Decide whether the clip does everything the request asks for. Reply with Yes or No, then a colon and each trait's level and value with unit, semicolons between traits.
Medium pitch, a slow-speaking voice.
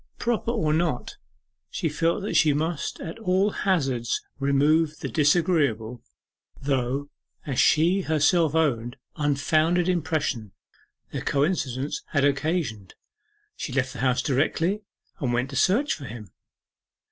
Yes: medium, 150 Hz; slow, 125 wpm